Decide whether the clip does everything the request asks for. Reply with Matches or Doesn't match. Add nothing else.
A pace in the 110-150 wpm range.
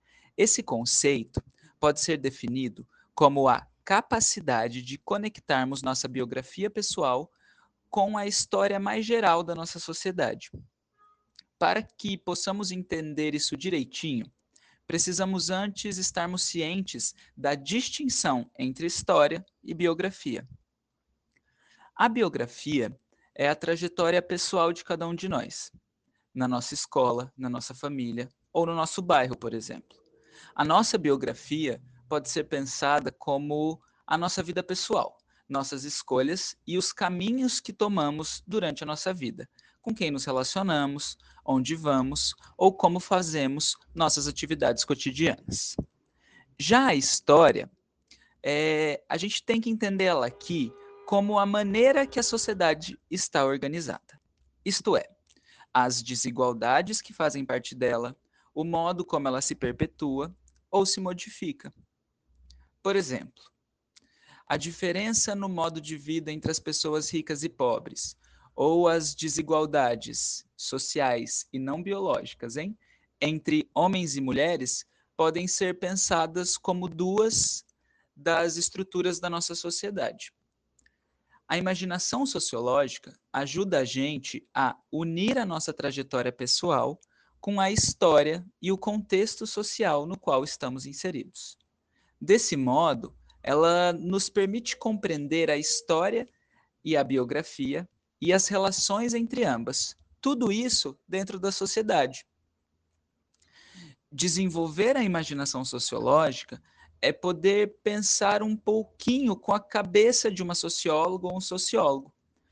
Matches